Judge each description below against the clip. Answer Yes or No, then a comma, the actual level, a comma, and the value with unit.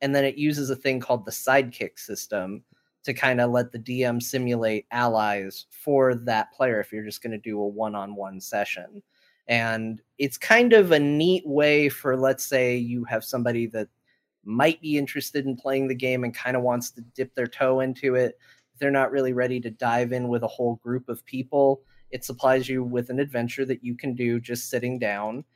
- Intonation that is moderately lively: No, narrow, 2.3 semitones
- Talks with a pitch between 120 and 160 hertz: Yes, low, 125 Hz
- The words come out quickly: Yes, fast, 210 wpm